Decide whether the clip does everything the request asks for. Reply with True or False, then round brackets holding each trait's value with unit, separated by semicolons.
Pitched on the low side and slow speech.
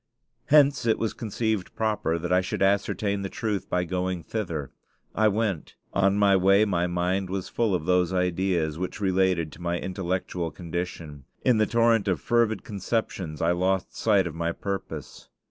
False (95 Hz; 170 wpm)